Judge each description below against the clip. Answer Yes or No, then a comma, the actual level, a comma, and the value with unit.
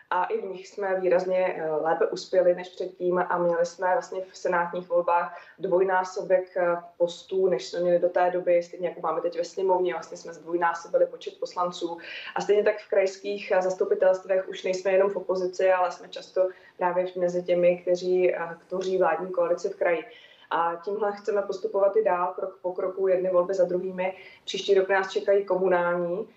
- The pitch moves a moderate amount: No, narrow, 1.5 semitones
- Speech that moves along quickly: Yes, fast, 175 wpm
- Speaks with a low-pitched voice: No, medium, 185 Hz